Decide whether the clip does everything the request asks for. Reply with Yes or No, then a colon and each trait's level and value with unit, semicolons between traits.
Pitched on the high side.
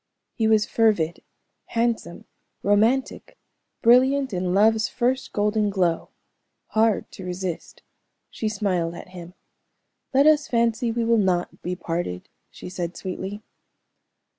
Yes: high, 210 Hz